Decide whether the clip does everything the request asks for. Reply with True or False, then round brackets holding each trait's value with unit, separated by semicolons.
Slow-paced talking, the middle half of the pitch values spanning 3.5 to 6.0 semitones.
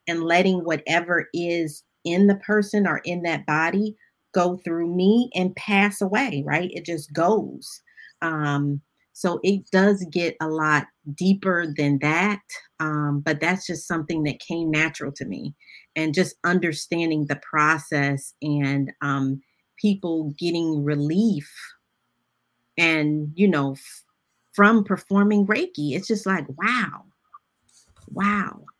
True (130 wpm; 4.3 semitones)